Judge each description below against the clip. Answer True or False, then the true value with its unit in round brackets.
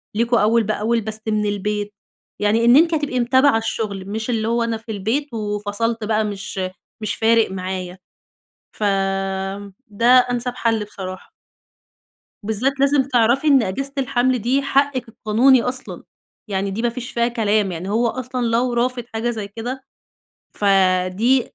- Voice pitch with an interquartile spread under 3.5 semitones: True (3.1 semitones)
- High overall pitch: True (230 Hz)